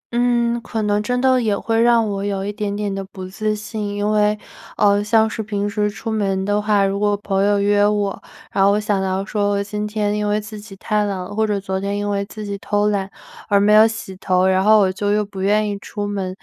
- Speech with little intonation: Yes, narrow, 1.2 semitones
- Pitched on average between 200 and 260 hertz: Yes, high, 205 Hz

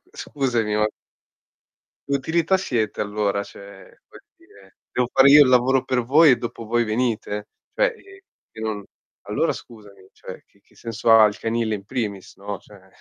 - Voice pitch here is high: No, low, 115 Hz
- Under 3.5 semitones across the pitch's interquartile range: No, average, 4.0 semitones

